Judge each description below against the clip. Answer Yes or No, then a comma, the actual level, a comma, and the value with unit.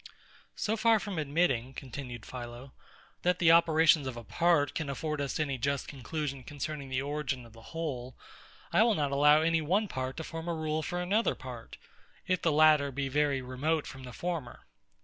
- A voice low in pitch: No, medium, 150 Hz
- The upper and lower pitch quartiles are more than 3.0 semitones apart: Yes, average, 3.7 semitones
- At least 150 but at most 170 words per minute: No, average, 190 wpm